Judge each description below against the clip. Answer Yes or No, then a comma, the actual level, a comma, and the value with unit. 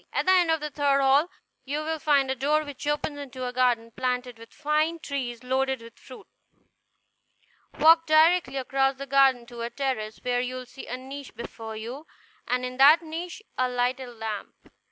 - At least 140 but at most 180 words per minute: No, average, 190 wpm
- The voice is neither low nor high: No, very high, 265 Hz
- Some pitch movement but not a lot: Yes, average, 3.1 semitones